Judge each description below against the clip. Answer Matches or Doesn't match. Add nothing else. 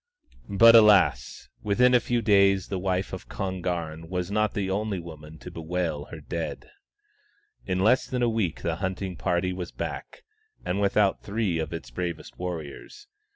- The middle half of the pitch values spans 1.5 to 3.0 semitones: Doesn't match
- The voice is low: Matches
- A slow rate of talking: Doesn't match